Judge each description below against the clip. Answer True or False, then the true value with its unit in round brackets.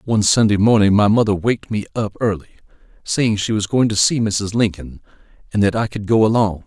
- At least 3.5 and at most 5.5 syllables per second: False (5.8 syllables/s)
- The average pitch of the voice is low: True (105 Hz)